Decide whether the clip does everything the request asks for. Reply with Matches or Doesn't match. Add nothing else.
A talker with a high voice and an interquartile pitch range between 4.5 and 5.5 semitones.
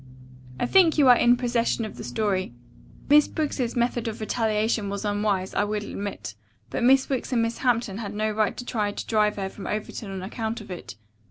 Doesn't match